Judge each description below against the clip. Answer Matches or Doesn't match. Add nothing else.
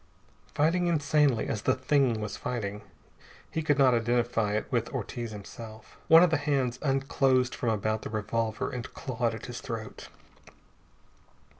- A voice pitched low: Matches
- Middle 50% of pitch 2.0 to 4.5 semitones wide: Matches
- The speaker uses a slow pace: Doesn't match